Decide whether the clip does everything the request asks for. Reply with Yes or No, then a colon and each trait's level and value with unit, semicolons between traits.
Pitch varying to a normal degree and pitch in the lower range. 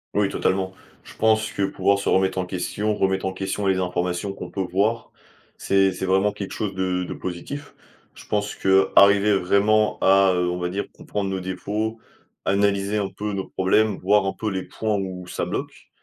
No: narrow, 1.7 semitones; very low, 95 Hz